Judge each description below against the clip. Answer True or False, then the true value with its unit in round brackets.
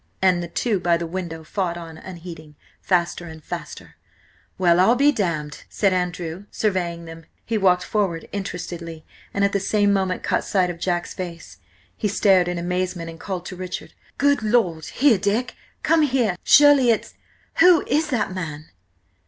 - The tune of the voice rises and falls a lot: False (3.4 semitones)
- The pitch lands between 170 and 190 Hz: True (185 Hz)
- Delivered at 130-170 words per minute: True (160 wpm)